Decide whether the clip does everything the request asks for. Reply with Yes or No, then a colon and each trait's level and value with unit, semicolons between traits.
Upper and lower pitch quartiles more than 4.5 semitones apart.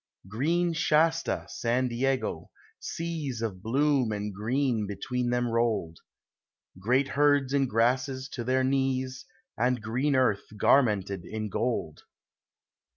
No: average, 3.6 semitones